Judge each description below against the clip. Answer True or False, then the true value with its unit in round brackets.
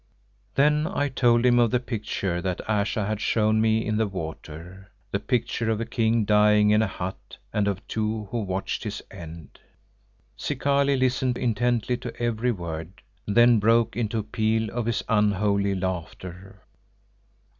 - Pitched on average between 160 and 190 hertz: False (110 Hz)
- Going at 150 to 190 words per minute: True (155 wpm)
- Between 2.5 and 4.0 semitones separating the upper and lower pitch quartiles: True (3.1 semitones)